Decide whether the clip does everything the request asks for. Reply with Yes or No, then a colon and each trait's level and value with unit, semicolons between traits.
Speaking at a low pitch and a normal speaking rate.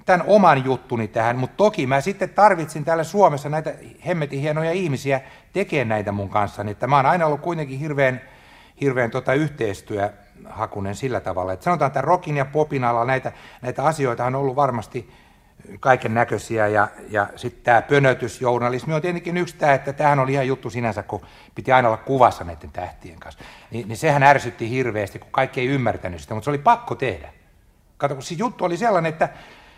No: low, 130 Hz; fast, 185 wpm